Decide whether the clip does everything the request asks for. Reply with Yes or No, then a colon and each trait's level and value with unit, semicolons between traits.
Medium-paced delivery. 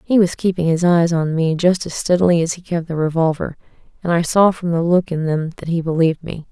No: fast, 250 wpm